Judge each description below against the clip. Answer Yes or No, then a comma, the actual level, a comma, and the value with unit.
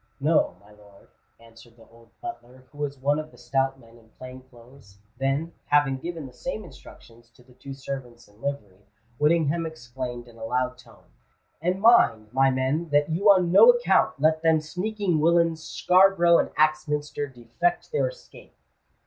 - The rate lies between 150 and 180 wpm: Yes, average, 170 wpm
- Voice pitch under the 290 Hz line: Yes, medium, 140 Hz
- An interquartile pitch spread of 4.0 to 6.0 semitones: Yes, average, 5.3 semitones